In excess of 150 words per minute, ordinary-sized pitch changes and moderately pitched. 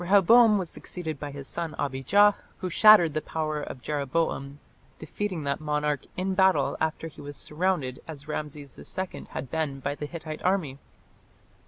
Yes: average, 165 wpm; average, 4.2 semitones; medium, 155 Hz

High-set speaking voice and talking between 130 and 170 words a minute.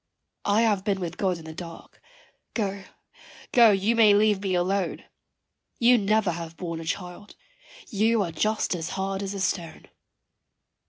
Yes: high, 195 Hz; average, 160 wpm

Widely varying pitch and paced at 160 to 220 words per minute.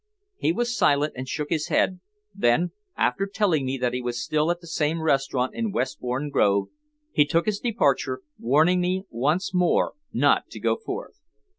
Yes: wide, 5.7 semitones; average, 175 wpm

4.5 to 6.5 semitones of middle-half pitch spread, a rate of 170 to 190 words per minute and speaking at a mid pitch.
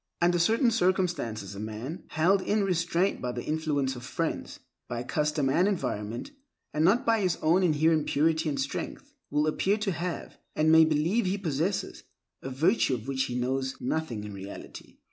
Yes: wide, 5.5 semitones; average, 175 wpm; medium, 155 Hz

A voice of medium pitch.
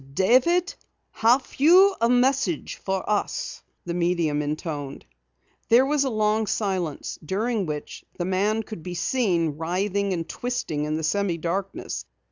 No: high, 195 Hz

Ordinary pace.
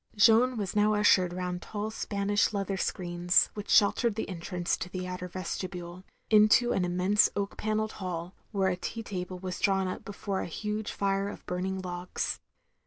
Yes: average, 180 wpm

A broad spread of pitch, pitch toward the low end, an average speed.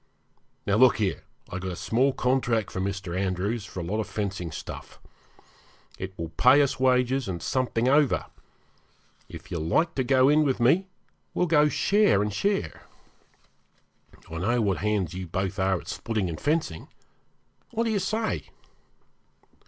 Yes: wide, 6.2 semitones; low, 110 Hz; average, 160 wpm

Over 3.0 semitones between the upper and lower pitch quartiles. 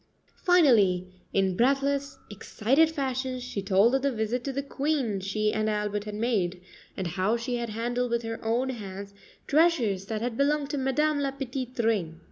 Yes: average, 4.7 semitones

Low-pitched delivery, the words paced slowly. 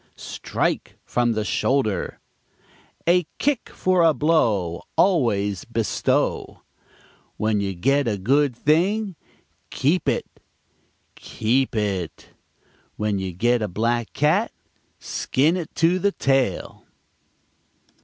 Yes: low, 125 Hz; slow, 105 wpm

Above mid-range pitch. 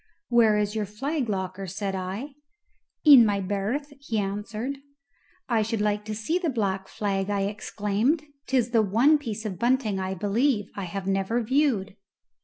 Yes: high, 210 Hz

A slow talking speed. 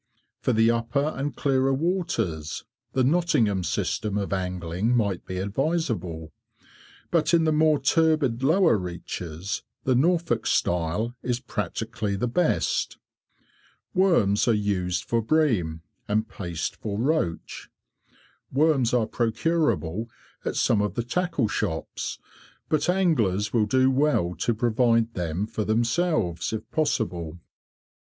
Yes: slow, 125 wpm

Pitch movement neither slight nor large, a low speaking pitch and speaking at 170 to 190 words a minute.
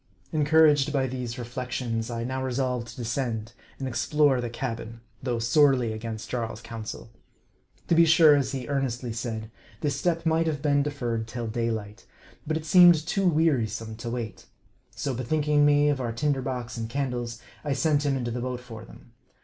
Yes: average, 3.9 semitones; low, 125 Hz; average, 180 wpm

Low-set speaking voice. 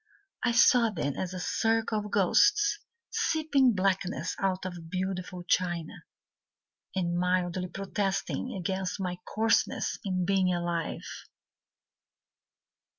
No: medium, 185 Hz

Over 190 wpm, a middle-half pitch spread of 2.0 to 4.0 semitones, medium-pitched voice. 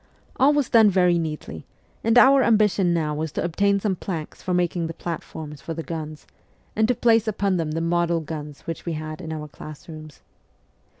No: average, 200 wpm; average, 4.4 semitones; medium, 170 Hz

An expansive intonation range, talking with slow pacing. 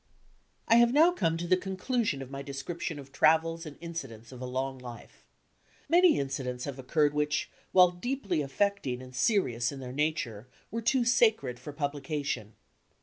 No: wide, 6.1 semitones; average, 170 wpm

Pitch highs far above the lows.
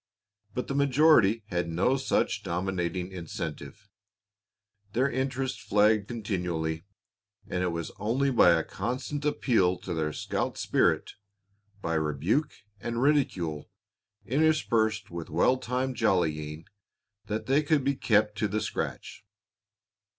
Yes: wide, 7.1 semitones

